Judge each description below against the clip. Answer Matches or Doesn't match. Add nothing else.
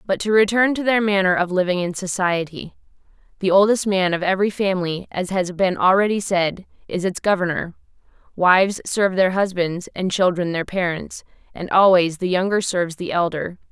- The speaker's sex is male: Doesn't match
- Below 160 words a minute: Doesn't match